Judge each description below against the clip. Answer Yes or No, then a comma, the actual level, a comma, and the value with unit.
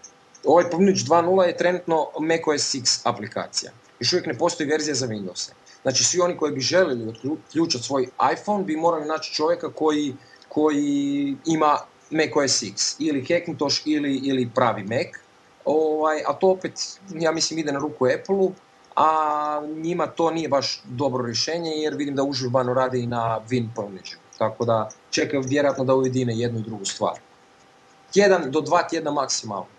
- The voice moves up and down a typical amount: Yes, average, 3.9 semitones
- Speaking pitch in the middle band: Yes, medium, 150 Hz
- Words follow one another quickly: Yes, fast, 165 wpm